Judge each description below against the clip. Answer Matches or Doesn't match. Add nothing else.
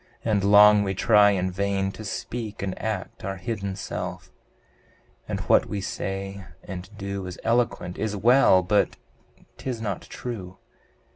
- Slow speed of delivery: Doesn't match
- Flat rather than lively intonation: Matches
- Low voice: Matches